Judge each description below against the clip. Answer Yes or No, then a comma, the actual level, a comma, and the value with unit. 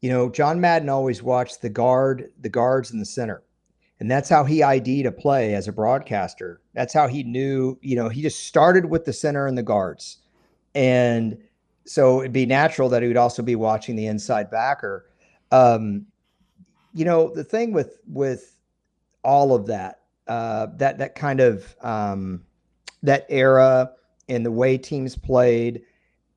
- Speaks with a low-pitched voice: Yes, low, 130 Hz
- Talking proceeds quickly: No, average, 170 wpm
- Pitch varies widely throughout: No, average, 2.9 semitones